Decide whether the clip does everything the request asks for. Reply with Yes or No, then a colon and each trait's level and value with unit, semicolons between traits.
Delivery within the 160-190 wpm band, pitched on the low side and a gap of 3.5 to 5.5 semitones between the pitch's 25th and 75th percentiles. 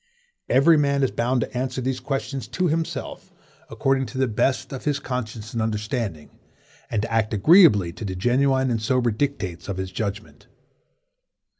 Yes: average, 165 wpm; low, 125 Hz; average, 4.0 semitones